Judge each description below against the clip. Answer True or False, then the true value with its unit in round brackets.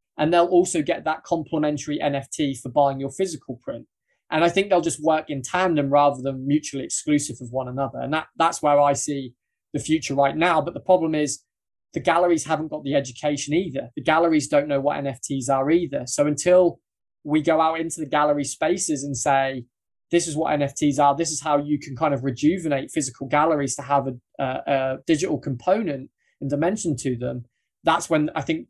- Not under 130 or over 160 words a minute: False (205 wpm)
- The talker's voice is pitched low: False (150 Hz)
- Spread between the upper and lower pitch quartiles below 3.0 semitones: True (2.6 semitones)